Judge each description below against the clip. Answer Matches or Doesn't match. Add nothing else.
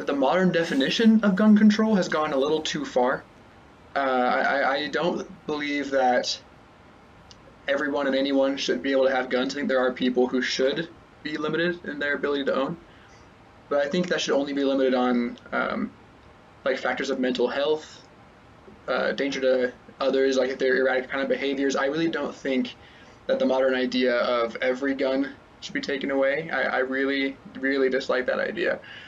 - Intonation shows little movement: Matches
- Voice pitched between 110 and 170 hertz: Matches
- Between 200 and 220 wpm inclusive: Doesn't match